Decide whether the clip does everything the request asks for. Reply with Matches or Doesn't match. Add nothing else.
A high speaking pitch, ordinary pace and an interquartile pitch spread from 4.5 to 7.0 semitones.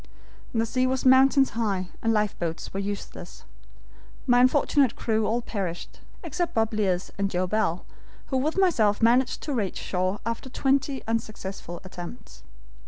Matches